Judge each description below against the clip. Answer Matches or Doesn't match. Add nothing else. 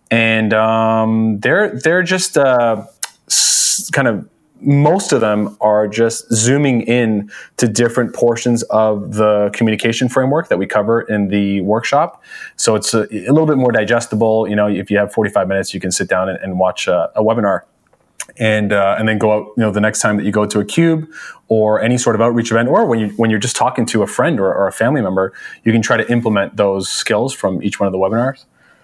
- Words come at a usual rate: Doesn't match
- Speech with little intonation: Matches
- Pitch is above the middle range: Doesn't match